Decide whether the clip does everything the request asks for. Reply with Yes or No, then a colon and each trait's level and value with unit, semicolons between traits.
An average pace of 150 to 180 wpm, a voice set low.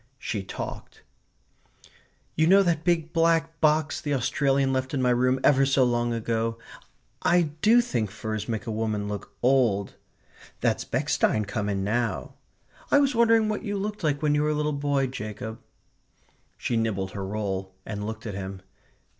Yes: average, 170 wpm; low, 125 Hz